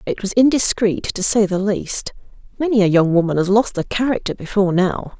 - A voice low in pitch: No, high, 200 Hz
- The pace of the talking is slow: No, average, 195 wpm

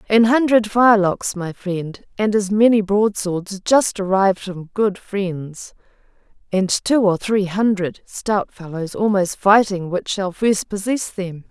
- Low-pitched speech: No, high, 200 Hz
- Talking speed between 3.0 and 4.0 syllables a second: Yes, 3.9 syllables/s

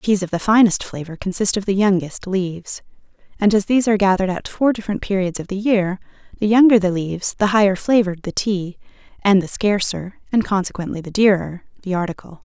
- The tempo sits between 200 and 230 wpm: No, average, 190 wpm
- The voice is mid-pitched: No, high, 195 Hz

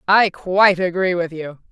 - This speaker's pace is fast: No, average, 175 wpm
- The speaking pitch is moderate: Yes, medium, 180 Hz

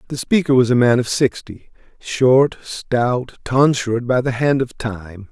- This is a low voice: Yes, low, 125 Hz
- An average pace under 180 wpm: Yes, average, 170 wpm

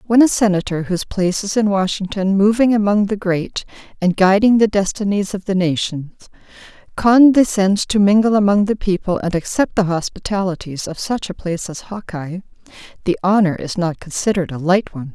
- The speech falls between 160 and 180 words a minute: Yes, average, 170 wpm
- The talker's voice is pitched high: Yes, high, 195 Hz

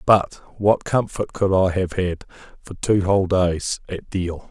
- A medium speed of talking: Yes, average, 175 wpm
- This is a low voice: Yes, very low, 95 Hz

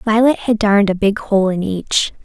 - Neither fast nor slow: No, fast, 215 wpm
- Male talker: No, female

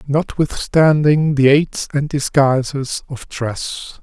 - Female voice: No, male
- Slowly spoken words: Yes, slow, 105 wpm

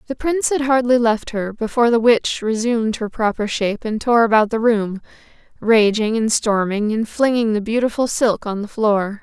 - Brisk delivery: No, average, 190 wpm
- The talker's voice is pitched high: Yes, high, 225 Hz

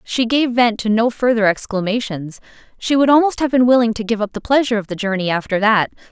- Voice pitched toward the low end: No, high, 225 Hz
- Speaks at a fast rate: Yes, fast, 225 wpm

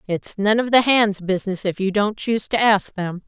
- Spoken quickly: Yes, fast, 240 wpm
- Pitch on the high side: Yes, high, 205 Hz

